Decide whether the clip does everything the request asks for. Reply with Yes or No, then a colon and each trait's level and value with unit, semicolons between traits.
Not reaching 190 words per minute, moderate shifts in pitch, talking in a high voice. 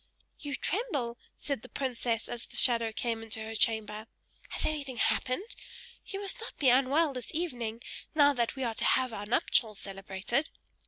Yes: average, 170 wpm; average, 4.0 semitones; high, 245 Hz